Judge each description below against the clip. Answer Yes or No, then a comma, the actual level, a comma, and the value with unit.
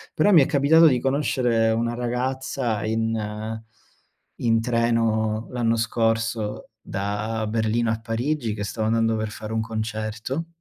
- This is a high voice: No, low, 115 Hz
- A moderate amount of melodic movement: No, narrow, 1.8 semitones